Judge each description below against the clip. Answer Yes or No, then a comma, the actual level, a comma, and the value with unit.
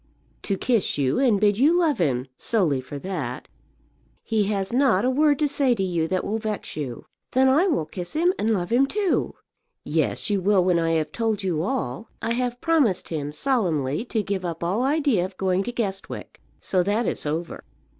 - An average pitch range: No, wide, 6.4 semitones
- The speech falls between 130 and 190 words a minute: No, average, 200 wpm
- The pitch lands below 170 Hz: No, high, 205 Hz